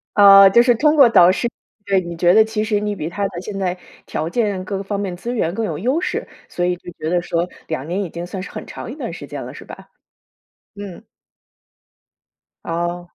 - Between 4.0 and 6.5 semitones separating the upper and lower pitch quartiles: No, average, 3.3 semitones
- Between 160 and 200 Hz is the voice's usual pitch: Yes, high, 190 Hz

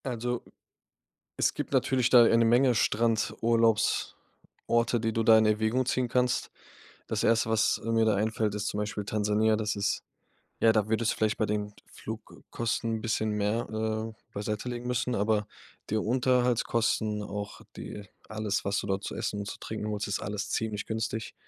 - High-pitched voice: No, low, 110 Hz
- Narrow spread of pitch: Yes, narrow, 1.8 semitones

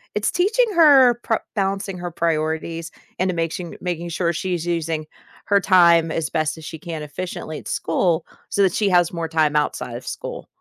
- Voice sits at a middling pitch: Yes, medium, 170 Hz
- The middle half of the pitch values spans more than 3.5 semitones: No, average, 3.0 semitones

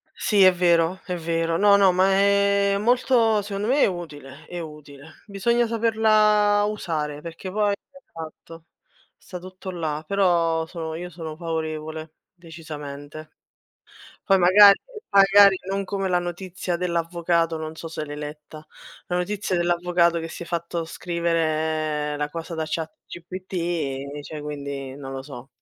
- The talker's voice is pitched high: No, medium, 170 Hz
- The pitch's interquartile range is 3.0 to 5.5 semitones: Yes, average, 3.6 semitones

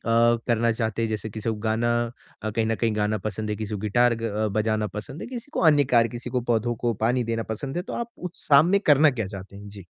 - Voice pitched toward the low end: Yes, low, 115 Hz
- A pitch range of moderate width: No, narrow, 2.2 semitones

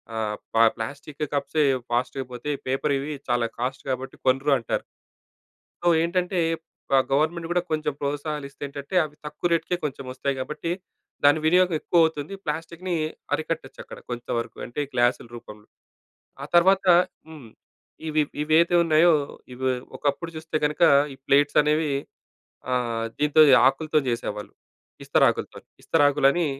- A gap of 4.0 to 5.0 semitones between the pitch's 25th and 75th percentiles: No, average, 3.3 semitones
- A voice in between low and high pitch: Yes, medium, 145 Hz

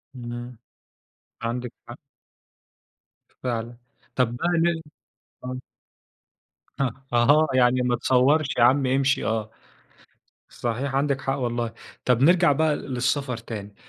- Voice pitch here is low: Yes, low, 125 Hz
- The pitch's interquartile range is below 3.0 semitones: Yes, narrow, 2.6 semitones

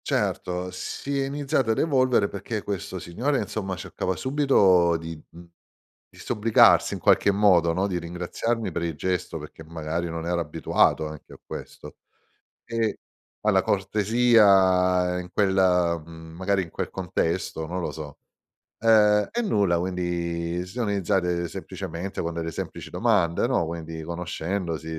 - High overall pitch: No, very low, 90 Hz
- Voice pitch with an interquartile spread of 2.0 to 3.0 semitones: No, average, 3.7 semitones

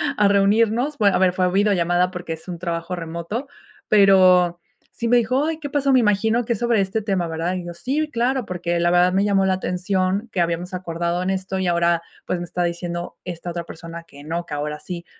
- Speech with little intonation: No, average, 3.3 semitones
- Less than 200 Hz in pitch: Yes, medium, 185 Hz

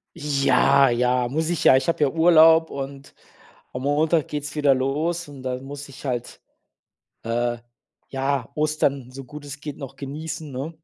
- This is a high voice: No, medium, 140 Hz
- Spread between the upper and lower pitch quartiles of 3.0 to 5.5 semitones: No, narrow, 2.5 semitones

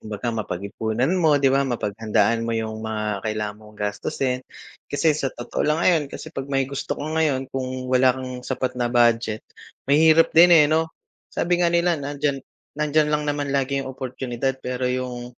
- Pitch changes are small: No, average, 4.0 semitones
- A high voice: No, low, 130 Hz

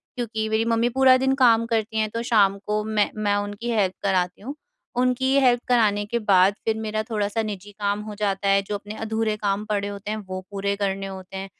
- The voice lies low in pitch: No, high, 210 Hz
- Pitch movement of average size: No, narrow, 2.0 semitones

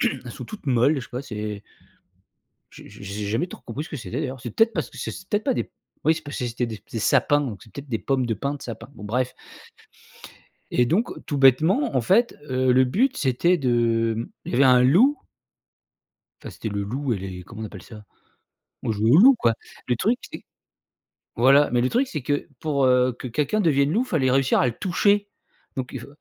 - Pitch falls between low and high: No, low, 130 Hz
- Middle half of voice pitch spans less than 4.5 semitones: No, average, 4.9 semitones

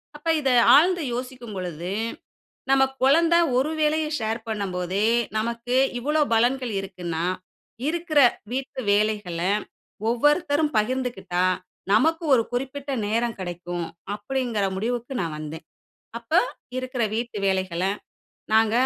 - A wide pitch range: Yes, wide, 5.7 semitones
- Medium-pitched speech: No, high, 235 Hz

